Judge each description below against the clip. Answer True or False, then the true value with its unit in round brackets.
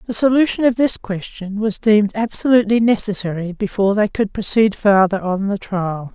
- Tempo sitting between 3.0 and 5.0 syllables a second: False (5.4 syllables/s)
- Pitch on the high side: True (210 Hz)